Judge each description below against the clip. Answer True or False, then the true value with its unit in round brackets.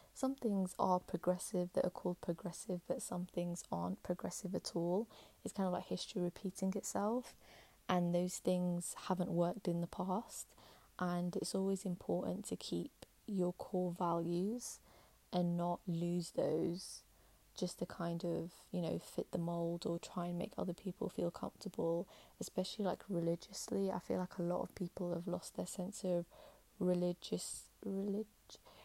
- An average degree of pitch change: False (1.7 semitones)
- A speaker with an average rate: True (160 wpm)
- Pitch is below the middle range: False (180 Hz)